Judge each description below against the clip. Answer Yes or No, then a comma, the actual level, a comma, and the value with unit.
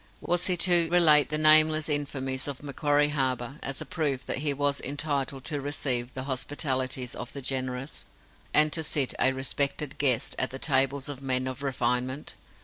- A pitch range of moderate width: No, narrow, 2.3 semitones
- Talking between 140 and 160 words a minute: No, average, 175 wpm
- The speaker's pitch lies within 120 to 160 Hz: Yes, medium, 140 Hz